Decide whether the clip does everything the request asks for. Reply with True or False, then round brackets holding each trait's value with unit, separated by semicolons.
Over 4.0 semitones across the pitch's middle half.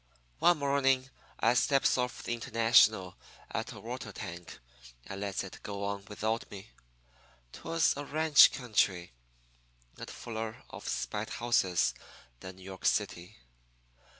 True (5.0 semitones)